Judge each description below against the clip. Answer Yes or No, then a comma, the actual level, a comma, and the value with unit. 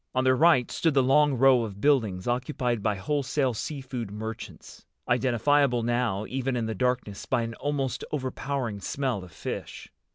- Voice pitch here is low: Yes, low, 125 Hz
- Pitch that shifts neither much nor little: Yes, average, 3.2 semitones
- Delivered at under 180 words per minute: Yes, average, 160 wpm